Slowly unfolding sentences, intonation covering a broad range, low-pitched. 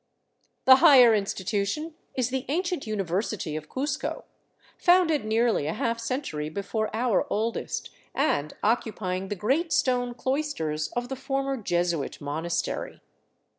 No: slow, 125 wpm; wide, 6.2 semitones; high, 230 Hz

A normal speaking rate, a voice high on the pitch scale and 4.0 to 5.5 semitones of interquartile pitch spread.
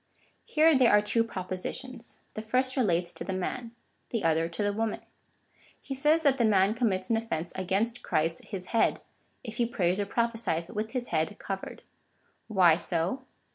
Yes: average, 175 wpm; high, 215 Hz; average, 4.3 semitones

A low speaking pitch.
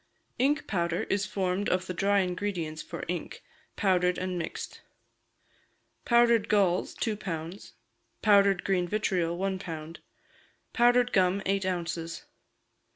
No: medium, 185 Hz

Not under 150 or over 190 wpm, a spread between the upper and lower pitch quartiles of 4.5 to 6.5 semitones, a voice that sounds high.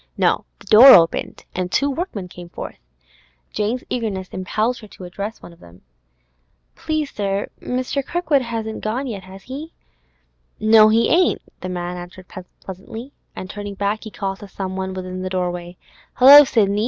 Yes: average, 165 wpm; average, 4.9 semitones; high, 205 Hz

